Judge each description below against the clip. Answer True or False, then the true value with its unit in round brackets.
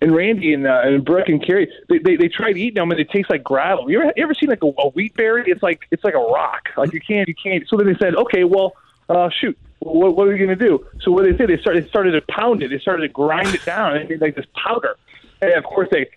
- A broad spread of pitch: True (5.7 semitones)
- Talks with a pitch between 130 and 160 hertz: False (190 Hz)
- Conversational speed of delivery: False (295 wpm)